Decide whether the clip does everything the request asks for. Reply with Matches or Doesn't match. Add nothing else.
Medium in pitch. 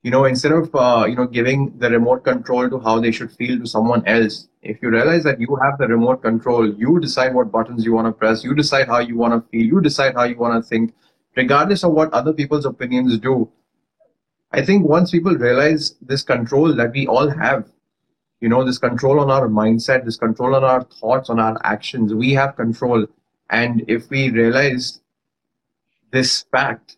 Doesn't match